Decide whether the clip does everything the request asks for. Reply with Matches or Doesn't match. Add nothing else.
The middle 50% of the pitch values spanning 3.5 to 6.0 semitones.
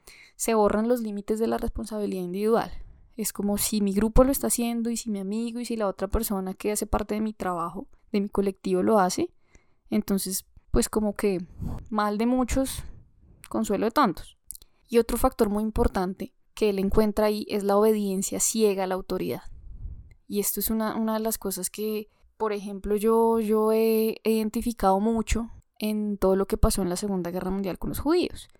Doesn't match